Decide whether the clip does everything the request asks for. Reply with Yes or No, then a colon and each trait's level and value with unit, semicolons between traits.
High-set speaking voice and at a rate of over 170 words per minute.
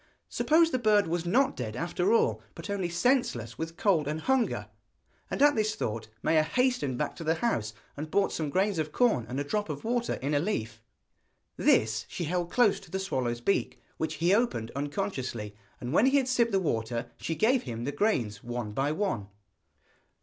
No: medium, 165 Hz; average, 195 wpm